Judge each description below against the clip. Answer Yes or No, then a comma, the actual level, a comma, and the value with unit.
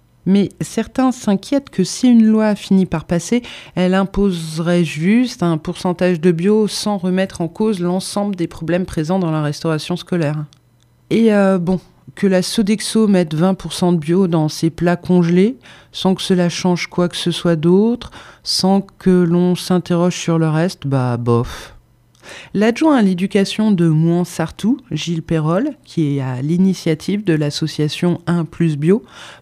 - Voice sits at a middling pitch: Yes, medium, 180 Hz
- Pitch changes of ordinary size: Yes, average, 3.0 semitones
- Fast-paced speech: No, average, 160 wpm